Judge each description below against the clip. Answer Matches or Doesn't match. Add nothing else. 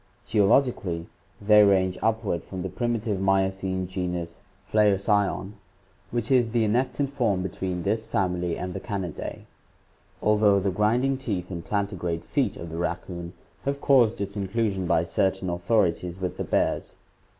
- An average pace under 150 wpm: Matches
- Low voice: Matches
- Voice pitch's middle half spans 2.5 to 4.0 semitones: Matches